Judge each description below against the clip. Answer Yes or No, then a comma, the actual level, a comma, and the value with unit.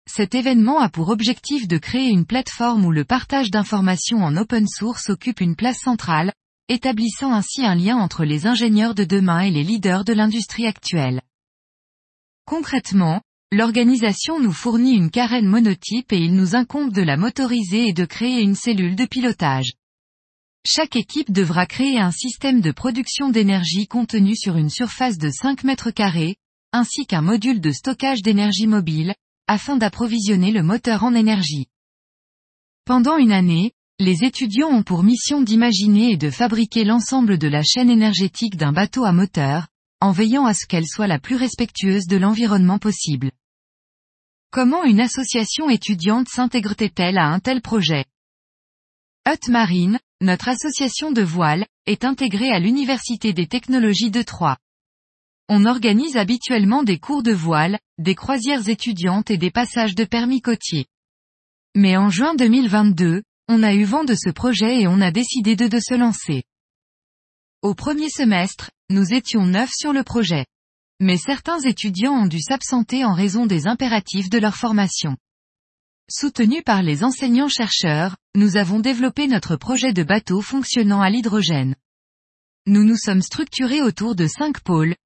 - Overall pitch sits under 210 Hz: No, high, 220 Hz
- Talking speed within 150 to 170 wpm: Yes, average, 155 wpm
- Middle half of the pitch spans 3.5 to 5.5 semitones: Yes, average, 4.7 semitones